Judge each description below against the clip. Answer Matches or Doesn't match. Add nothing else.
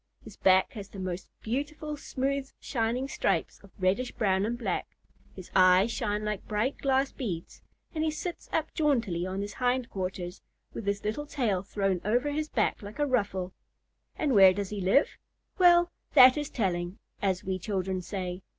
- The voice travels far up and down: Matches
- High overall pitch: Matches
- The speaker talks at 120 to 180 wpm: Matches